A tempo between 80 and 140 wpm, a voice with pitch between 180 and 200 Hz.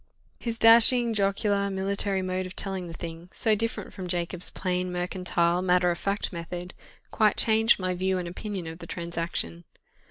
No: average, 165 wpm; medium, 185 Hz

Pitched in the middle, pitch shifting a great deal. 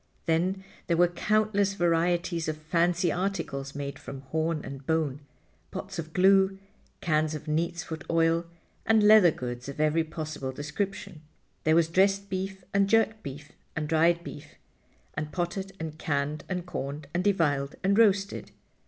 No: medium, 165 Hz; average, 3.9 semitones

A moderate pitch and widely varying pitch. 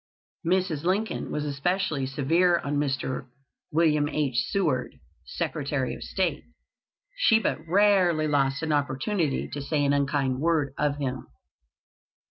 No: medium, 150 Hz; average, 3.8 semitones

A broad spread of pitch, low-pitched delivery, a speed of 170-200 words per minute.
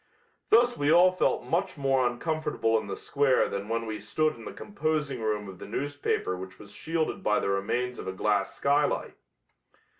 Yes: wide, 6.8 semitones; low, 125 Hz; average, 185 wpm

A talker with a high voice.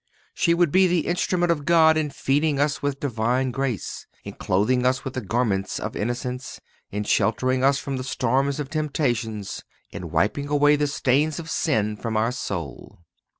No: low, 135 Hz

